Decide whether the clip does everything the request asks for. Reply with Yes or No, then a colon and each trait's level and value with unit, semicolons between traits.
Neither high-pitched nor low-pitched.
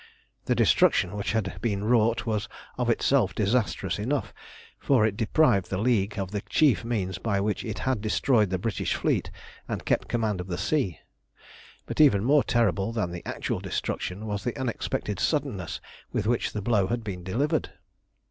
No: low, 110 Hz